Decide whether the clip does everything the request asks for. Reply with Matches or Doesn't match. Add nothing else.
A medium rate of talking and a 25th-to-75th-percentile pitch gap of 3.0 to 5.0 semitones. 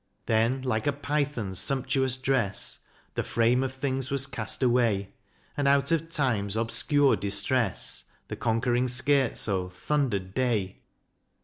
Doesn't match